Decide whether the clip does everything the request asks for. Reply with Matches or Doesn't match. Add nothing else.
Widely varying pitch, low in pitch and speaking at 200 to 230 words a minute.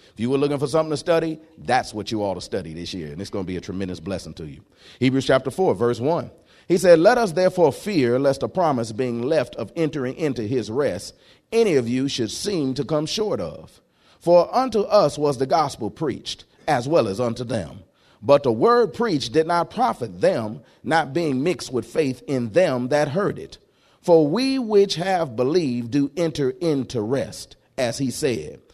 Doesn't match